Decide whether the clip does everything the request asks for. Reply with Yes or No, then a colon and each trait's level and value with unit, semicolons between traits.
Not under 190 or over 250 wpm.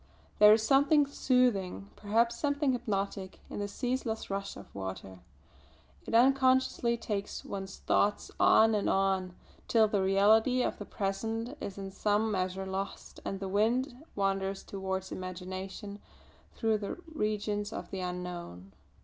No: average, 140 wpm